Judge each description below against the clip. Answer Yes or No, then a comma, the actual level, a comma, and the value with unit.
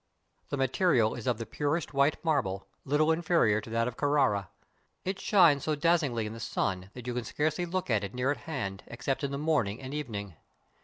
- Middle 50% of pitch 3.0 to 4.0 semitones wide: No, wide, 5.4 semitones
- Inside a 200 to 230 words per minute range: Yes, fast, 205 wpm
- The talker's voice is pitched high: No, low, 135 Hz